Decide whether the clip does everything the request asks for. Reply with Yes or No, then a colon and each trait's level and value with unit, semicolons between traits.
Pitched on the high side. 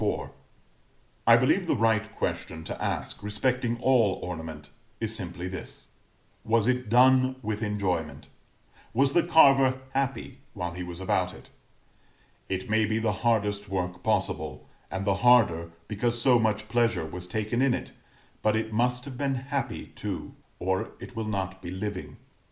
No: low, 110 Hz